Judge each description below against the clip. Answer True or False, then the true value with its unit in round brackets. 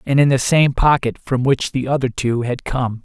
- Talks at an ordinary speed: False (235 wpm)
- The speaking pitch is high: False (130 Hz)